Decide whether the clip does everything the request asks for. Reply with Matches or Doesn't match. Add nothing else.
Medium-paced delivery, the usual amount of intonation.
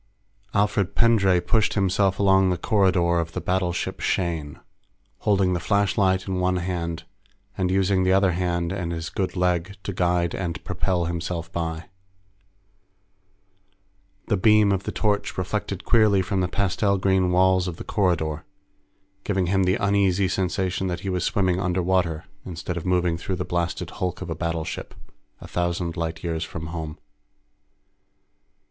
Doesn't match